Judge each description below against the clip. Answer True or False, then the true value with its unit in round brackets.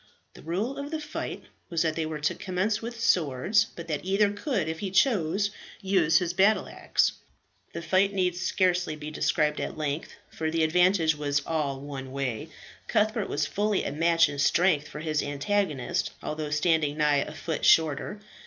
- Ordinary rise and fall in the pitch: True (4.4 semitones)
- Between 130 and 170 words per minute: False (180 wpm)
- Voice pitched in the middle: True (165 Hz)